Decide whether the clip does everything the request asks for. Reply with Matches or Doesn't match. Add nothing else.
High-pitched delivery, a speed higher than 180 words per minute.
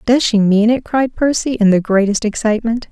Matches